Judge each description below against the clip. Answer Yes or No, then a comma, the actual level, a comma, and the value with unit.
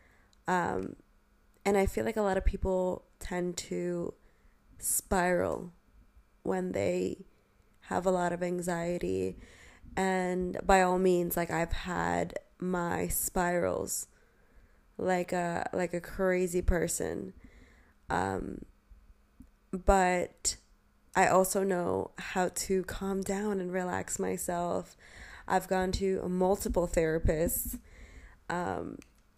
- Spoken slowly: Yes, slow, 105 wpm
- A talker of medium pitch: Yes, medium, 180 Hz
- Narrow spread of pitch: Yes, narrow, 1.4 semitones